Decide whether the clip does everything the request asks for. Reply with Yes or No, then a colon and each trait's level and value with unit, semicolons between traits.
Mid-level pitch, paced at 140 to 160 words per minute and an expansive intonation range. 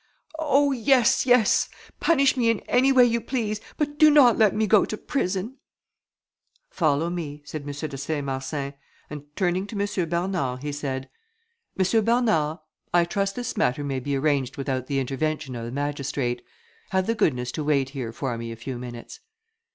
No: medium, 160 Hz; average, 175 wpm; wide, 8.2 semitones